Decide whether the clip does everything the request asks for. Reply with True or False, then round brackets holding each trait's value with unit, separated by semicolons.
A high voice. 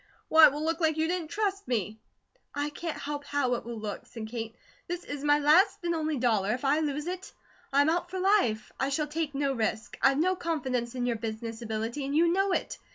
True (290 Hz)